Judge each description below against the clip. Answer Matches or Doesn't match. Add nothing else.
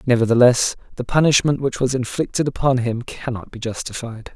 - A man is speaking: Matches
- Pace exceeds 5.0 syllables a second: Matches